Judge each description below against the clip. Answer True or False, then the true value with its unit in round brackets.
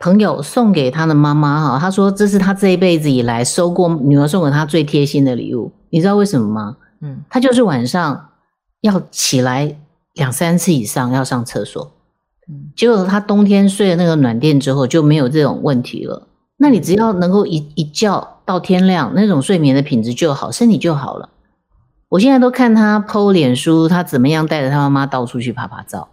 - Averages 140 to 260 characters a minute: False (295 characters per minute)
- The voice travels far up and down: True (6.0 semitones)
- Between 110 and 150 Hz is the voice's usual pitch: False (165 Hz)